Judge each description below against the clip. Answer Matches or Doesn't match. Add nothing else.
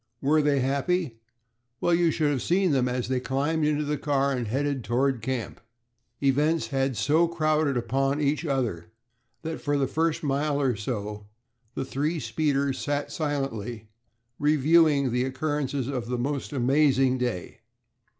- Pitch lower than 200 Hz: Matches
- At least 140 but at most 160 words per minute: Matches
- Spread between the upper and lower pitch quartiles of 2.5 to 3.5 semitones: Matches